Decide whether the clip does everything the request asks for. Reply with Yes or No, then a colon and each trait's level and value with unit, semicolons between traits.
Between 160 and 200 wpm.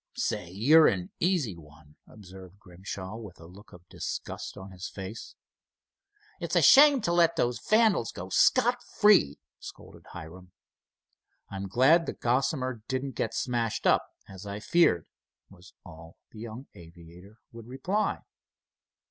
No: average, 140 wpm